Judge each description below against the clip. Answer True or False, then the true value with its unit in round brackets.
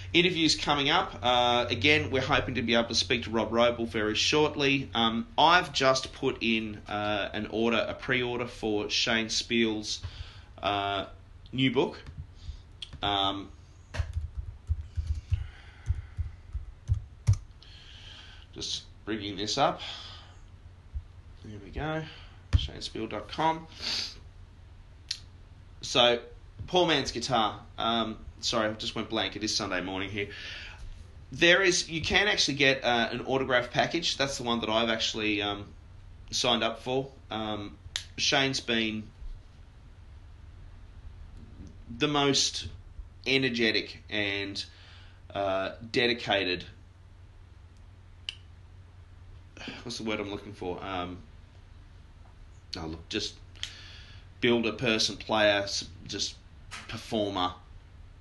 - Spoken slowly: True (105 wpm)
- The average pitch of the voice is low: True (100 Hz)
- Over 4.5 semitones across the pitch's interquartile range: False (4.2 semitones)